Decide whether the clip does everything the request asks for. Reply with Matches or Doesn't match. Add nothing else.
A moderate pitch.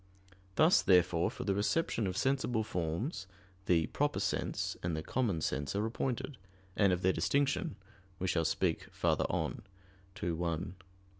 Doesn't match